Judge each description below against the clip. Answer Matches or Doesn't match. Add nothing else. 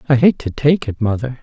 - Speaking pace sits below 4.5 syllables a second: Doesn't match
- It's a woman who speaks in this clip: Doesn't match